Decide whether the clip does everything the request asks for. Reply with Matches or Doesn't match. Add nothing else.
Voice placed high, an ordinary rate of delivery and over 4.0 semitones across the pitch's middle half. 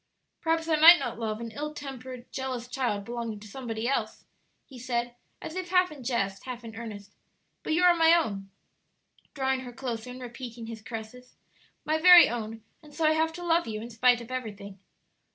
Matches